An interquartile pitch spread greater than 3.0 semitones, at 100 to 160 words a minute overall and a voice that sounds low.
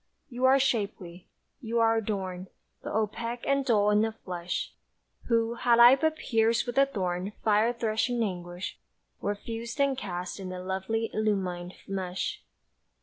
No: average, 3.9 semitones; average, 150 wpm; high, 220 Hz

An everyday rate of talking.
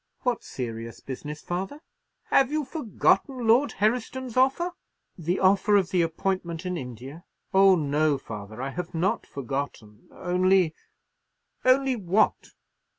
No: slow, 125 wpm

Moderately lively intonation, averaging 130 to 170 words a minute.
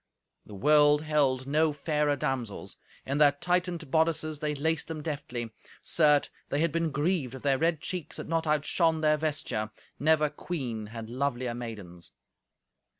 Yes: average, 3.5 semitones; average, 150 wpm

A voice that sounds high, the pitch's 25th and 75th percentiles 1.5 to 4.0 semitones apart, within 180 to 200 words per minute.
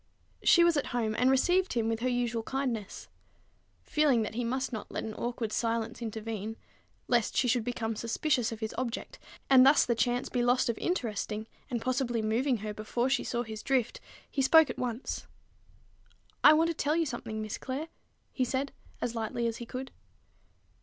Yes: high, 240 Hz; average, 2.9 semitones; average, 185 wpm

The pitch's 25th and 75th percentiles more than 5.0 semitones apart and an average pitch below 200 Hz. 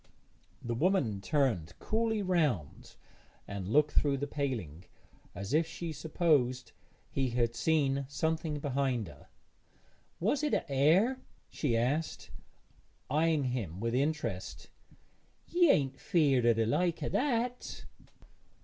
Yes: wide, 5.6 semitones; medium, 140 Hz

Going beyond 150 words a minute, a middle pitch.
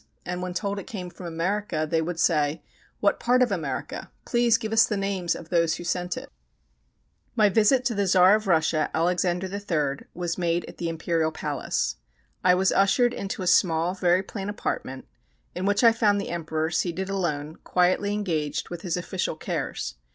Yes: average, 185 wpm; medium, 180 Hz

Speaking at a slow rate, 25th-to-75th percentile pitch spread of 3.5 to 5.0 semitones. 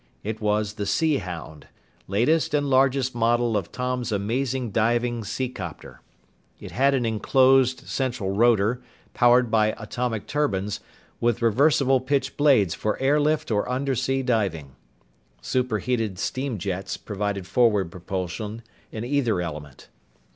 Yes: slow, 125 wpm; average, 4.2 semitones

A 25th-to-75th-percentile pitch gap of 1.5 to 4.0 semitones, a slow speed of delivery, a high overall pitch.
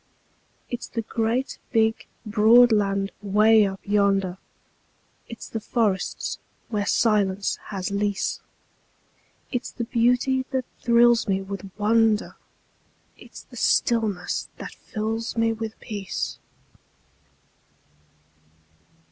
Yes: narrow, 2.4 semitones; slow, 100 wpm; high, 220 Hz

